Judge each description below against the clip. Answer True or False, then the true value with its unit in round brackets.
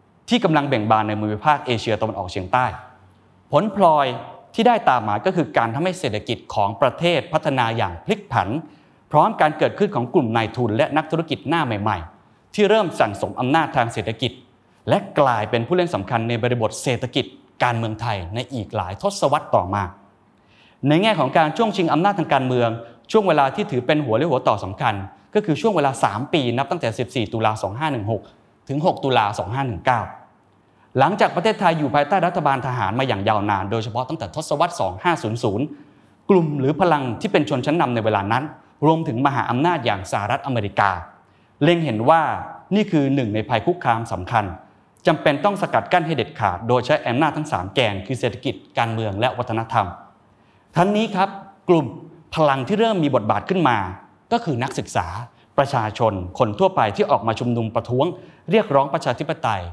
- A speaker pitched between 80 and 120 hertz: False (130 Hz)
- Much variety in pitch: True (6.2 semitones)